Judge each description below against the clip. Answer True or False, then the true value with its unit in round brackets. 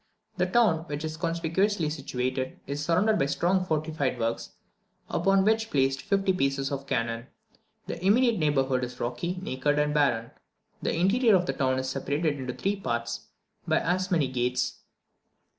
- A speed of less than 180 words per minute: True (160 wpm)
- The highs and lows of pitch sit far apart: True (5.8 semitones)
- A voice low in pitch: False (150 Hz)